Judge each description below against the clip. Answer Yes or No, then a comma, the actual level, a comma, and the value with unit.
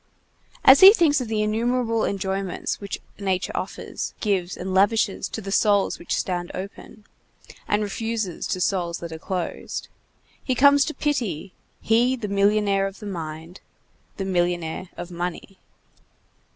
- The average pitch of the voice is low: No, high, 200 Hz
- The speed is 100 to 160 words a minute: Yes, average, 140 wpm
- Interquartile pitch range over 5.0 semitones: No, average, 3.7 semitones